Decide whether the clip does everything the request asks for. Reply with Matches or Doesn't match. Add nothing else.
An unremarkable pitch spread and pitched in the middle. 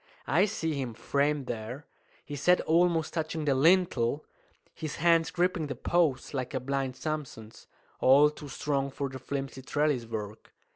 Matches